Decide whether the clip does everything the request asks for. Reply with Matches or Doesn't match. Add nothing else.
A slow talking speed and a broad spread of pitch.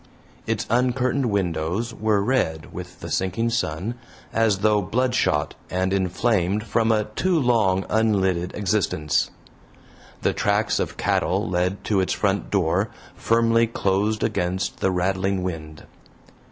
Doesn't match